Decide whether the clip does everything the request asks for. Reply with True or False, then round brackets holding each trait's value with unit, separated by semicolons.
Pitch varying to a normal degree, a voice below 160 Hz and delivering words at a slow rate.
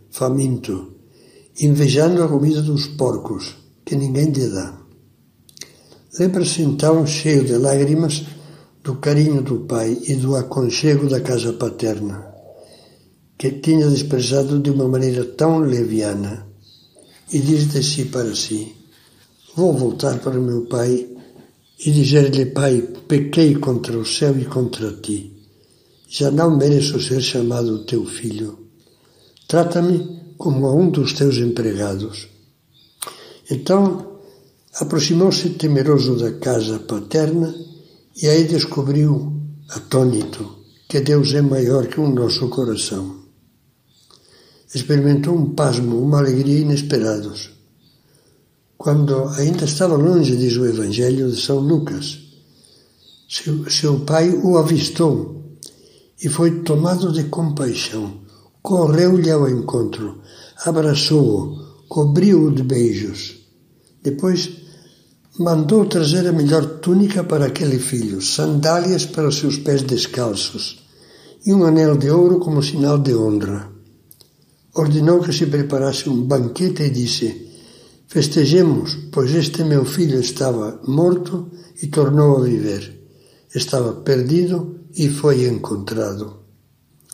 True (4.4 semitones; 140 Hz; 115 wpm)